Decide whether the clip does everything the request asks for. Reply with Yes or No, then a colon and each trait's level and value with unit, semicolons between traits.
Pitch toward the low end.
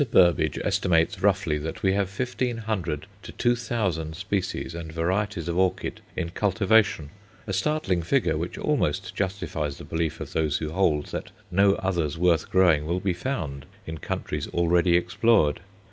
Yes: very low, 90 Hz